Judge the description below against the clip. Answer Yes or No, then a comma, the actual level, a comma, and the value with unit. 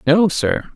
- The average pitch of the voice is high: No, medium, 165 Hz